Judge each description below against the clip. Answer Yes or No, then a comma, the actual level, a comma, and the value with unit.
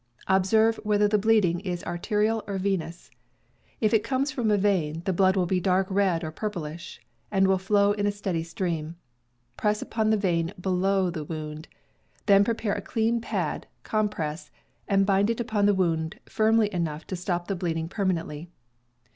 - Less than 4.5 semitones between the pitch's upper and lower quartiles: Yes, average, 3.5 semitones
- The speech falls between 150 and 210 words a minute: Yes, average, 170 wpm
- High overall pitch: Yes, high, 195 Hz